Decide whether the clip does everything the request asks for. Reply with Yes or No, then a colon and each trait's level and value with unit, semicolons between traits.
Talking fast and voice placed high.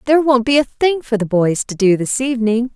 Yes: fast, 260 wpm; high, 240 Hz